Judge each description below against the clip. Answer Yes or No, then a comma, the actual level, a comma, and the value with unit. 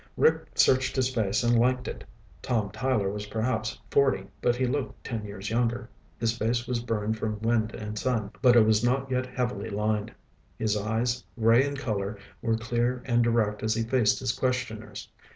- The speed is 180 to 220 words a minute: Yes, average, 185 wpm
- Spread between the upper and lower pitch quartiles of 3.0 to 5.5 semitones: No, narrow, 2.5 semitones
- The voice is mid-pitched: No, low, 115 Hz